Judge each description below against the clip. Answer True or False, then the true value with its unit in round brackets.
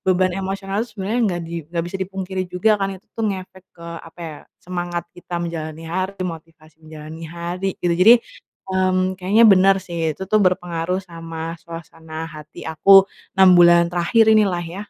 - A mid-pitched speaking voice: True (180 Hz)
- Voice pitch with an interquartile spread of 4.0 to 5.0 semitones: False (2.5 semitones)